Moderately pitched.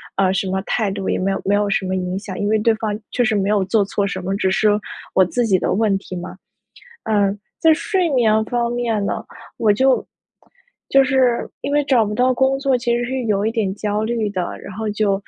No: high, 215 Hz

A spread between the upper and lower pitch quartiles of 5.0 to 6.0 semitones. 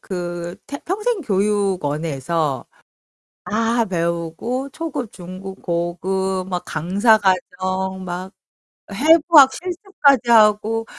Yes: wide, 5.5 semitones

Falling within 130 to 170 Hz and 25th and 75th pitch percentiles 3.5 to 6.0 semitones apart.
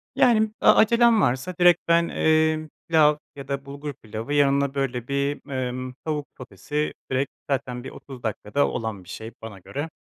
Yes: medium, 140 Hz; average, 3.9 semitones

